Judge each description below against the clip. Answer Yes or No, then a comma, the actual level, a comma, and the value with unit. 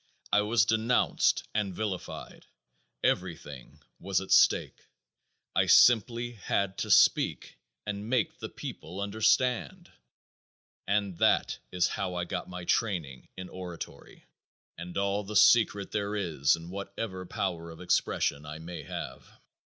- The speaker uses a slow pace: Yes, slow, 130 wpm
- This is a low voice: Yes, low, 100 Hz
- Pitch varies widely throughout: No, average, 3.3 semitones